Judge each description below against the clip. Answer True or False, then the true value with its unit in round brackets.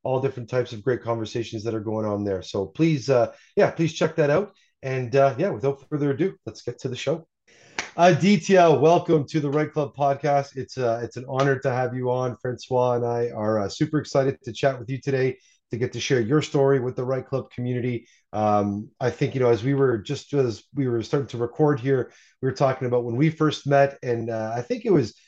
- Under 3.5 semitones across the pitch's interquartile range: True (3.1 semitones)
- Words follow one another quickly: True (235 wpm)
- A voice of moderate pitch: False (130 Hz)